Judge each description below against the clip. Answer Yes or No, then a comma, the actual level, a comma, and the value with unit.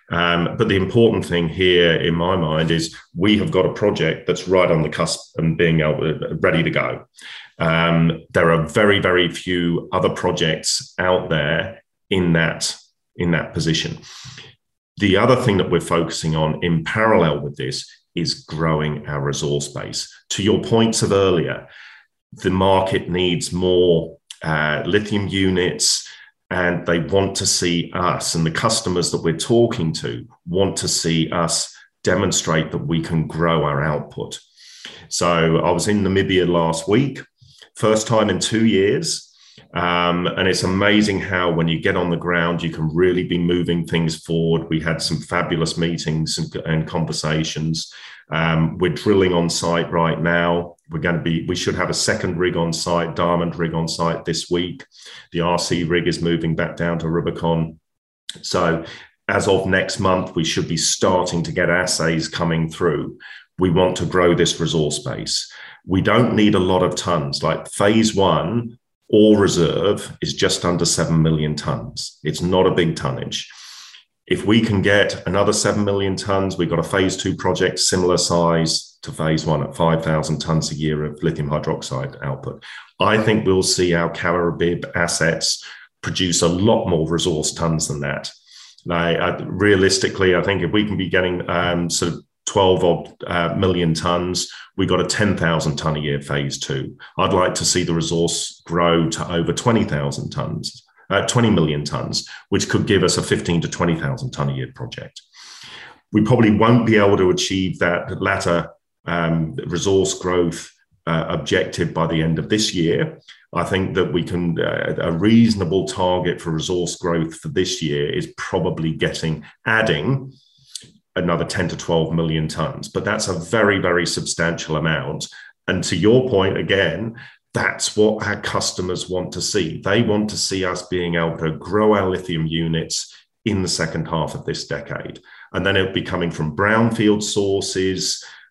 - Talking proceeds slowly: No, average, 170 wpm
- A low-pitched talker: Yes, very low, 85 Hz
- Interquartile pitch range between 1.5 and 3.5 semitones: Yes, narrow, 2.5 semitones